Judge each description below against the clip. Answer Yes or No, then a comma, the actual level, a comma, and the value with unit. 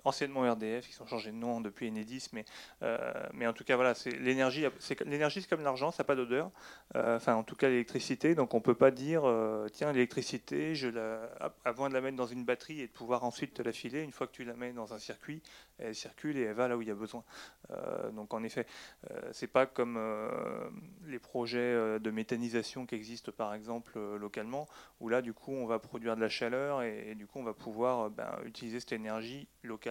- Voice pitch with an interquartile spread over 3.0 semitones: No, narrow, 2.6 semitones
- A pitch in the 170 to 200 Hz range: No, low, 120 Hz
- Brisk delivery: Yes, fast, 245 wpm